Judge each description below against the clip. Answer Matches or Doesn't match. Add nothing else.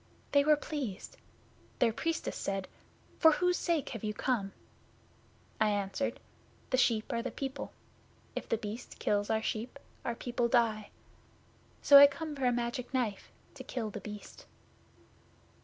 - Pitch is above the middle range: Matches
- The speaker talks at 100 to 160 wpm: Matches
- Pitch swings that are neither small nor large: Matches